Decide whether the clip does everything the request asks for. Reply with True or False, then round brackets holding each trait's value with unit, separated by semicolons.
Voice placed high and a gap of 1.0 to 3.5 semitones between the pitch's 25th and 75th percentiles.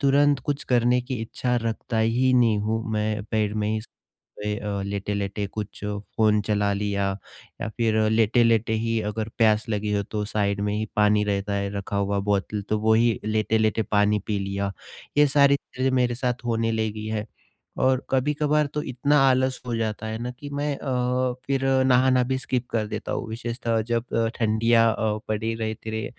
False (110 Hz; 2.9 semitones)